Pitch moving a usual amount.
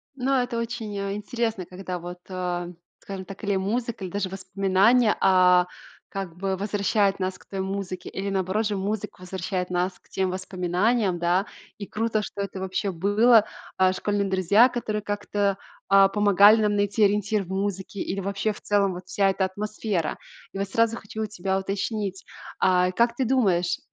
No: narrow, 2.1 semitones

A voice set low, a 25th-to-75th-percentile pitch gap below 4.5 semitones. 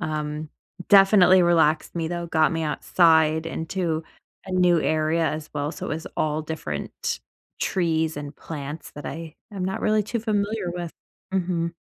No: medium, 165 Hz; narrow, 2.5 semitones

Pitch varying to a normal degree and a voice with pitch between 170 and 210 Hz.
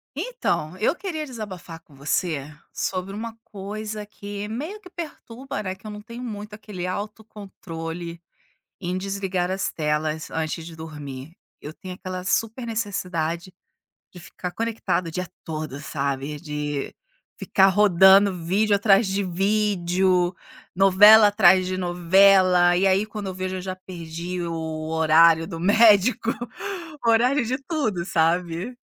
Yes: average, 3.9 semitones; medium, 185 Hz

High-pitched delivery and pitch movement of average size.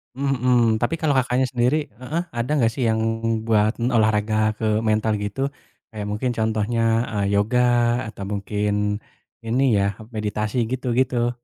No: low, 115 Hz; average, 3.1 semitones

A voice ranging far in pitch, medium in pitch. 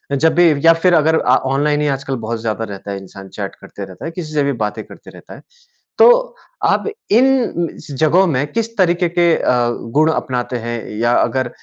Yes: wide, 6.2 semitones; medium, 145 Hz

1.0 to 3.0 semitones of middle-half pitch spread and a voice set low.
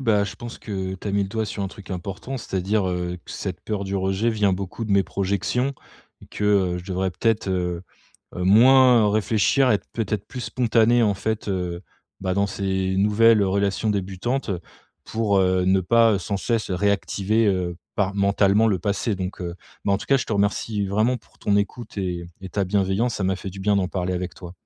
Yes: narrow, 2.6 semitones; low, 100 Hz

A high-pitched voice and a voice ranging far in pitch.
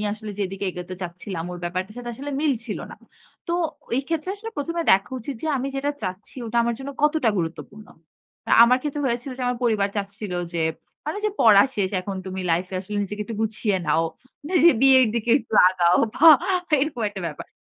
Yes: high, 220 Hz; wide, 6.1 semitones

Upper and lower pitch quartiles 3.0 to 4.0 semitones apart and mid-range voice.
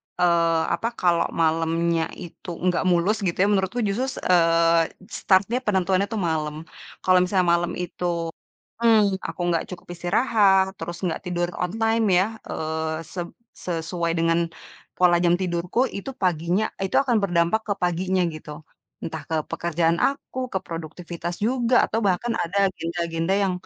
No: narrow, 2.5 semitones; medium, 175 Hz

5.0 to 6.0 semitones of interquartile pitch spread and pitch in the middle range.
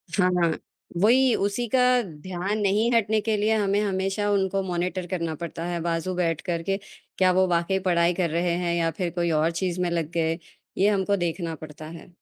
No: average, 2.8 semitones; medium, 180 Hz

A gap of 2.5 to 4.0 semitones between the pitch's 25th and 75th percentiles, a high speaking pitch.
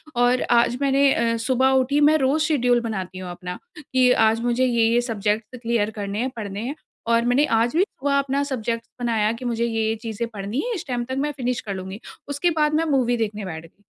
Yes: average, 3.3 semitones; high, 240 Hz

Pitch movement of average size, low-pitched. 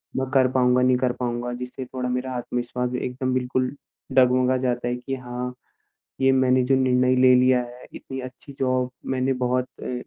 No: narrow, 0.6 semitones; low, 125 Hz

